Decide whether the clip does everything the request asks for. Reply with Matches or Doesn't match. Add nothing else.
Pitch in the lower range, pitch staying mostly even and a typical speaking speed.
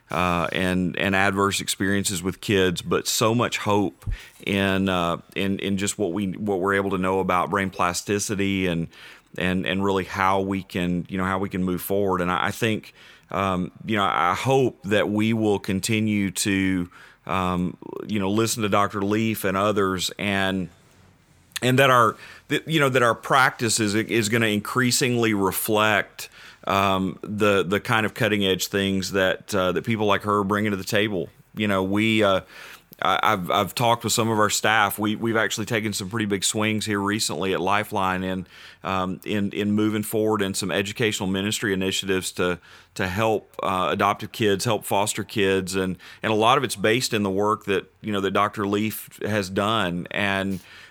Matches